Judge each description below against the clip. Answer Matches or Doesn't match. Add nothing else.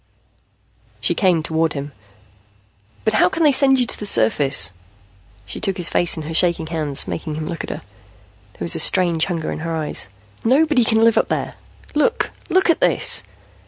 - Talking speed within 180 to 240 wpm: Matches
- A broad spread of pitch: Matches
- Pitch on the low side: Doesn't match